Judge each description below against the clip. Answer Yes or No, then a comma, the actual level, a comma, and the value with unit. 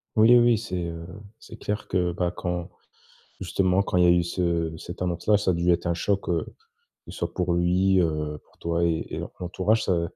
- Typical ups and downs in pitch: No, narrow, 1.9 semitones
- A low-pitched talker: Yes, very low, 90 Hz